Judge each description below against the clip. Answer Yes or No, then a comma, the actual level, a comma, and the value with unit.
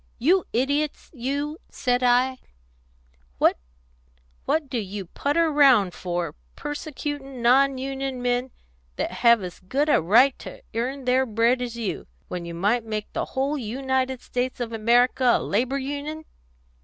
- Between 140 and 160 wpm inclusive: Yes, average, 145 wpm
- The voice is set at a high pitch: Yes, very high, 250 Hz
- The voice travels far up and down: No, average, 4.1 semitones